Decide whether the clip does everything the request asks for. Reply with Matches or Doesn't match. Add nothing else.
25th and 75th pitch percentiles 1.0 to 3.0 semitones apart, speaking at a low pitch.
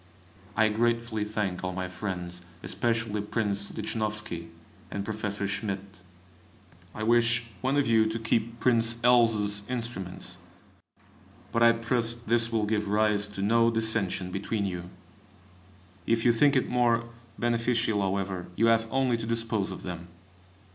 Matches